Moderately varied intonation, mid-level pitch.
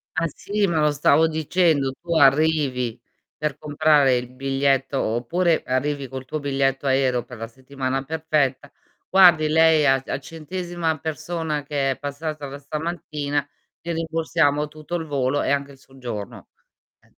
Yes: average, 3.0 semitones; medium, 145 Hz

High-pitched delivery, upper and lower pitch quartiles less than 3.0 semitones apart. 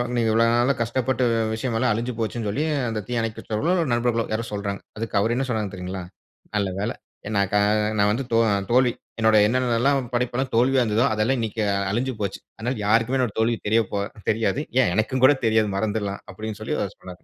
No: low, 115 Hz; narrow, 2.5 semitones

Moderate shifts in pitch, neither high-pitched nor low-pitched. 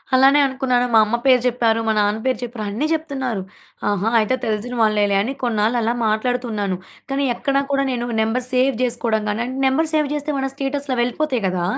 No: average, 3.6 semitones; high, 245 Hz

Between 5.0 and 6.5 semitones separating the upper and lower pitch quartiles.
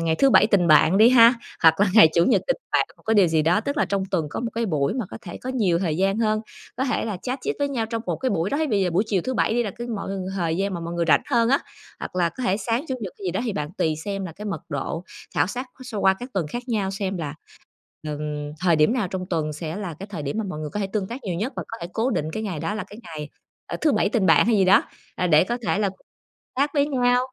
Yes: wide, 5.5 semitones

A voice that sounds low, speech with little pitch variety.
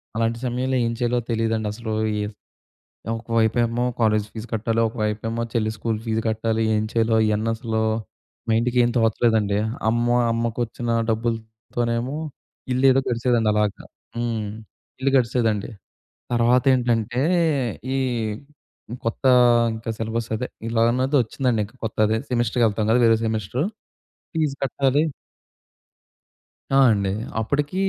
Yes: low, 115 Hz; narrow, 1.7 semitones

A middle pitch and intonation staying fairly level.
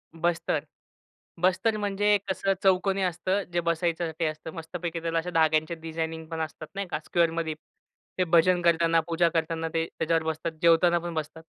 Yes: medium, 165 Hz; narrow, 1.6 semitones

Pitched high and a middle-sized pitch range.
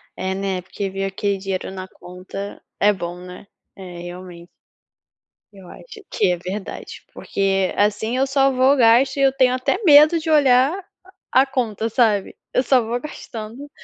No: high, 215 Hz; wide, 5.8 semitones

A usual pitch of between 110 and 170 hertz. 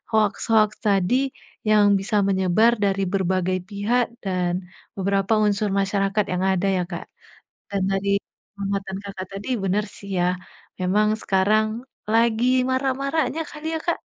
No: high, 200 Hz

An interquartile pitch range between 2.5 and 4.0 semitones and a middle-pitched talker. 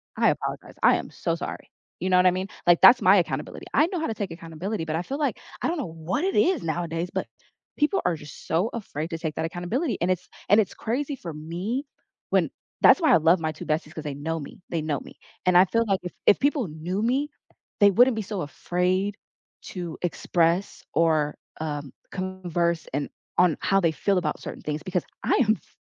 No: average, 4.6 semitones; medium, 180 Hz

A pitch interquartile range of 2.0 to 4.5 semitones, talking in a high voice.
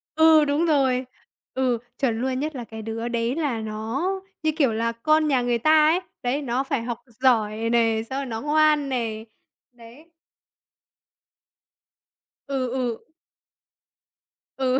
Yes: average, 3.9 semitones; very high, 255 Hz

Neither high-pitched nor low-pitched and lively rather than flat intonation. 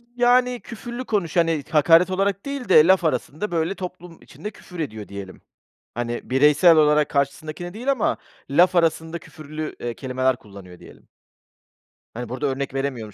Yes: medium, 160 Hz; wide, 5.9 semitones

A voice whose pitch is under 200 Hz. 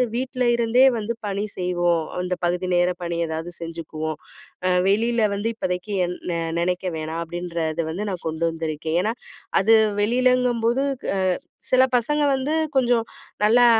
Yes: medium, 185 Hz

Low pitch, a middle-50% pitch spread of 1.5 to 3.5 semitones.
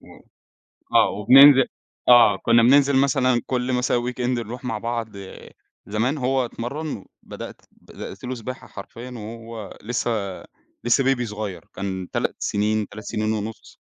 Yes: low, 120 Hz; average, 2.9 semitones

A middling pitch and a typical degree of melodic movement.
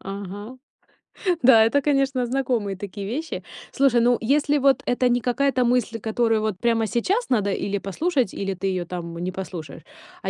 No: high, 230 Hz; average, 4.7 semitones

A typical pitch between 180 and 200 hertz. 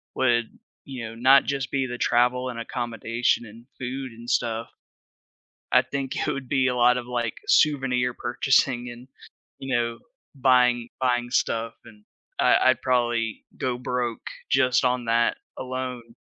No: low, 125 Hz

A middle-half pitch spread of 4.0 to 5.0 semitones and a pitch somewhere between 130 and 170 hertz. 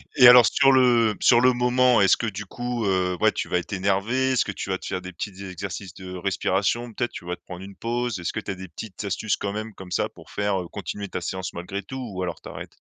No: average, 4.4 semitones; low, 100 Hz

